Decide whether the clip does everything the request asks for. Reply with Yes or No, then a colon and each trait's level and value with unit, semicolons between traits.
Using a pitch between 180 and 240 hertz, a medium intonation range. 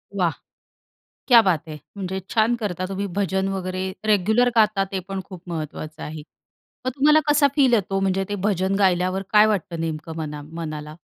Yes: high, 190 Hz; average, 3.8 semitones